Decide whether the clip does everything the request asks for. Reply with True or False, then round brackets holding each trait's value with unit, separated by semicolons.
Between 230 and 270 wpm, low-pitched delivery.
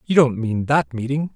False (220 wpm; 130 Hz)